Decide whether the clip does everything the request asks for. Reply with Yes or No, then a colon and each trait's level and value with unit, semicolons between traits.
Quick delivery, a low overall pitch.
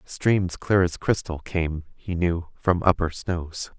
No: average, 160 wpm; very low, 90 Hz